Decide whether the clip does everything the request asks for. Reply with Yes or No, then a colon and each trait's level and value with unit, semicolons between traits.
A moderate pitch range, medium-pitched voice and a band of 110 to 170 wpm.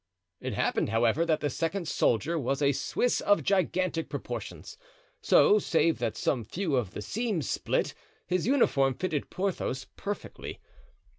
No: wide, 6.1 semitones; medium, 165 Hz; average, 145 wpm